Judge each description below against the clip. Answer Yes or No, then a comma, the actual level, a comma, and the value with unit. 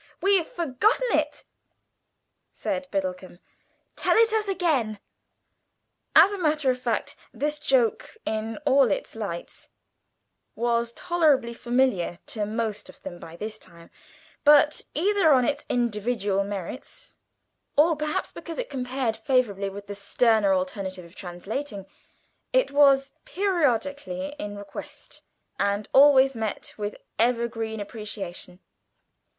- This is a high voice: Yes, high, 240 Hz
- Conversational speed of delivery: No, slow, 120 wpm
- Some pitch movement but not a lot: No, wide, 6.1 semitones